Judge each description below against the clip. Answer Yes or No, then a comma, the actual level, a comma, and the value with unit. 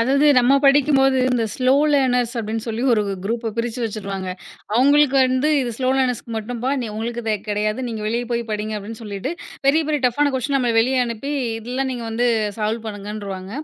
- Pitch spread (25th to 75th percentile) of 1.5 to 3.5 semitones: Yes, average, 3.2 semitones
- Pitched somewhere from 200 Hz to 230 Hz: No, high, 240 Hz